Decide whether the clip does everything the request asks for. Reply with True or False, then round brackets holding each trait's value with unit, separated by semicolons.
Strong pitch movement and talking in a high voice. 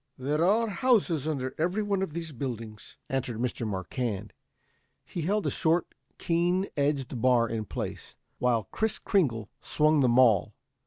False (6.6 semitones; 140 Hz)